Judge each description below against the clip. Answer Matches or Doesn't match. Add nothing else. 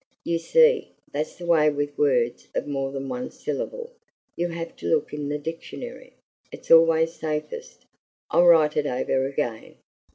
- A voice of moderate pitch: Matches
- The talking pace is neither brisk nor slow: Matches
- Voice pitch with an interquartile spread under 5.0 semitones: Matches